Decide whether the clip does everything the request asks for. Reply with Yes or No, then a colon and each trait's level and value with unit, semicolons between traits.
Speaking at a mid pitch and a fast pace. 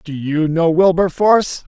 No: medium, 170 Hz; average, 140 wpm